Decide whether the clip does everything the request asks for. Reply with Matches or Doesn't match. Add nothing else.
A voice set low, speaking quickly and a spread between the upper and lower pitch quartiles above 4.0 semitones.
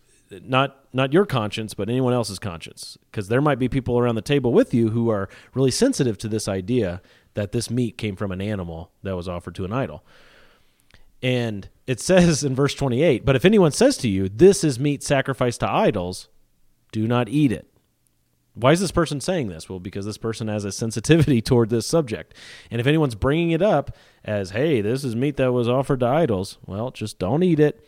Matches